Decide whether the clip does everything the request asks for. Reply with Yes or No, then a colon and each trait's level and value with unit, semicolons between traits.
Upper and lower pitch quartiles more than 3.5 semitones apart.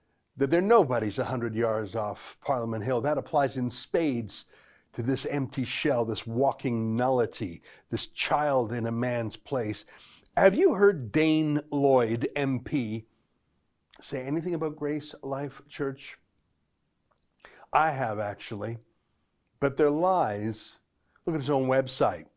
Yes: average, 4.1 semitones